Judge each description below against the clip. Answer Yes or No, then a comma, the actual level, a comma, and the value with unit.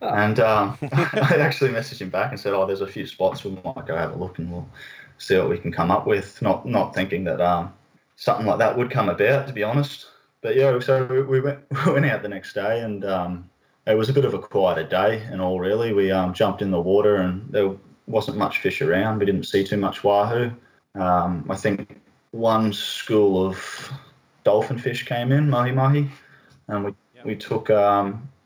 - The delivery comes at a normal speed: No, fast, 215 wpm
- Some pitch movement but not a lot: No, wide, 5.8 semitones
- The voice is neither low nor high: No, low, 110 Hz